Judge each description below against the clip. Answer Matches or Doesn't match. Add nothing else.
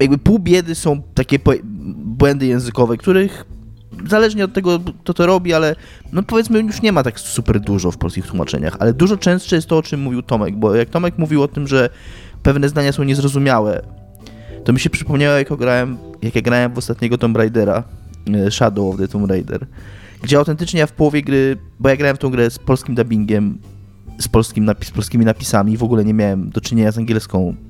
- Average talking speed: Doesn't match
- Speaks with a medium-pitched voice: Doesn't match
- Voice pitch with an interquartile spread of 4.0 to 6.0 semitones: Matches